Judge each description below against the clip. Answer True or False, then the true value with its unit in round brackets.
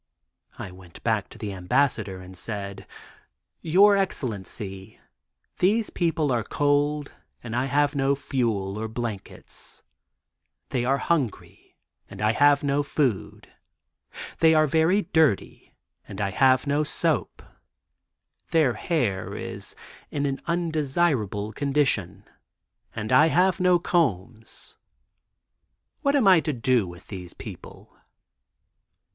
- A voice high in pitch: False (135 Hz)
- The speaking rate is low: True (120 wpm)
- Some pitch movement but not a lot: False (6.9 semitones)